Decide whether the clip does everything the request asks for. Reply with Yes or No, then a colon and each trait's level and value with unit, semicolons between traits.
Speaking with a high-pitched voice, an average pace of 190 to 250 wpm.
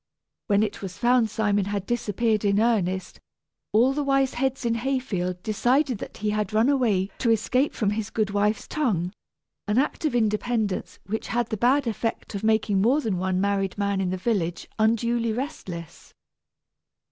No: high, 220 Hz; average, 170 wpm